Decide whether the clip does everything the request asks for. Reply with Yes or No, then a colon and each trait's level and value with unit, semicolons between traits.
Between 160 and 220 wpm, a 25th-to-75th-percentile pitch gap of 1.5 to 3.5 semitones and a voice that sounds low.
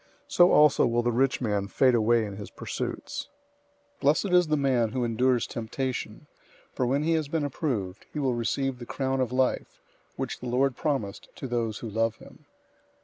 Yes: average, 190 wpm; average, 3.1 semitones; low, 125 Hz